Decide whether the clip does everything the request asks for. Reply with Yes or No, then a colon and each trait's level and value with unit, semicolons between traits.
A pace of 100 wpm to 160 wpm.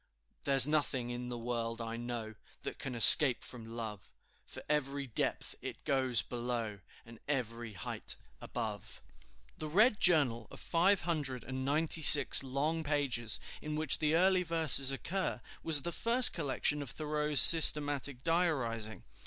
Yes: average, 145 wpm